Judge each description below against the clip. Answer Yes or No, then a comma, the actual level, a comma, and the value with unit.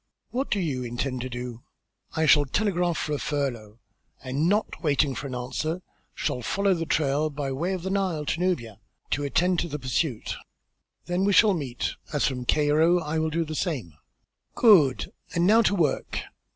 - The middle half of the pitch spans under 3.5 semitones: No, average, 5.1 semitones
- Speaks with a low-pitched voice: No, medium, 150 Hz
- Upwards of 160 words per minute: Yes, average, 185 wpm